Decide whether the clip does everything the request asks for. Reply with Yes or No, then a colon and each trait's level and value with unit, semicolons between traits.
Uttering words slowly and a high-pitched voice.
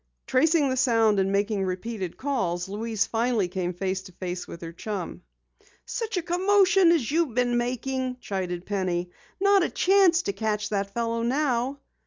No: average, 165 wpm; high, 230 Hz